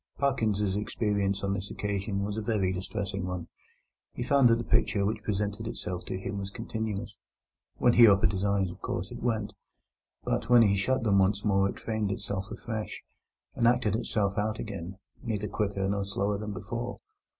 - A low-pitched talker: Yes, low, 100 Hz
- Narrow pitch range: Yes, narrow, 2.1 semitones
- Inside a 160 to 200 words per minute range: Yes, average, 185 wpm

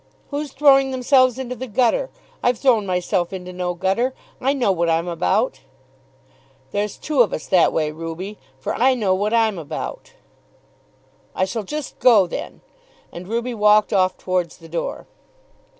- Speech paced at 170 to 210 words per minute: No, average, 160 wpm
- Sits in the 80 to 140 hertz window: No, high, 210 Hz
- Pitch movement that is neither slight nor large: No, wide, 6.0 semitones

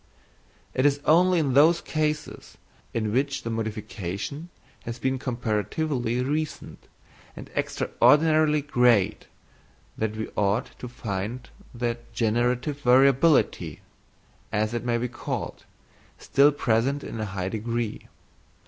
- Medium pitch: No, low, 125 Hz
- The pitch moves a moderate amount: Yes, average, 4.5 semitones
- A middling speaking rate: No, slow, 115 wpm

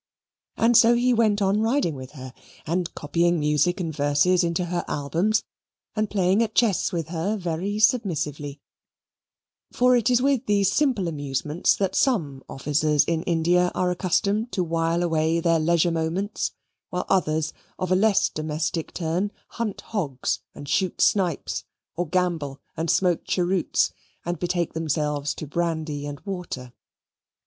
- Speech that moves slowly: No, average, 150 wpm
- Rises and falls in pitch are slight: No, average, 4.3 semitones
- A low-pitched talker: No, medium, 175 Hz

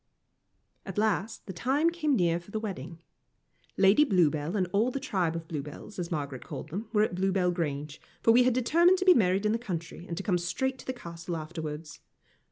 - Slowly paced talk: No, fast, 205 wpm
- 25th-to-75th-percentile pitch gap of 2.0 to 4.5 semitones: No, wide, 5.5 semitones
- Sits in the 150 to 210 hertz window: Yes, medium, 185 Hz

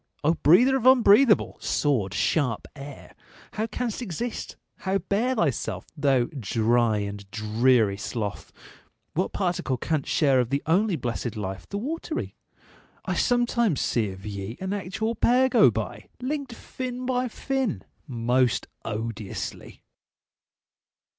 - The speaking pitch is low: No, medium, 150 Hz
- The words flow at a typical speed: No, slow, 125 wpm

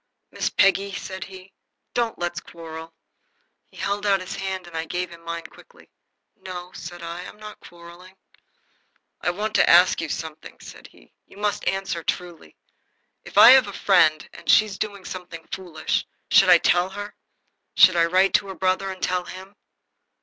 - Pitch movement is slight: Yes, narrow, 2.3 semitones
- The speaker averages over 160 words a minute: Yes, average, 175 wpm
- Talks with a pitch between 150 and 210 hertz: Yes, medium, 185 Hz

